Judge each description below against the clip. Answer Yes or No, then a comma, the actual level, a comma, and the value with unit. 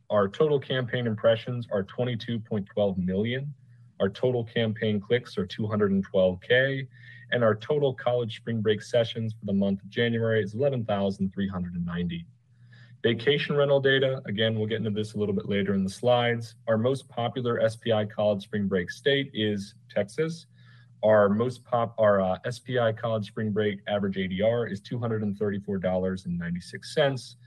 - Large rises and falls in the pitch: No, average, 3.2 semitones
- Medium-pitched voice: No, low, 110 Hz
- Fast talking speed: No, average, 140 wpm